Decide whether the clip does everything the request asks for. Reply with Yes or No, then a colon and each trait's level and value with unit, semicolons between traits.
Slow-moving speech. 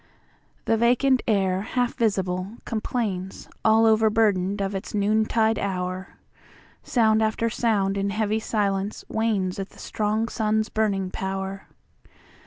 Yes: slow, 105 wpm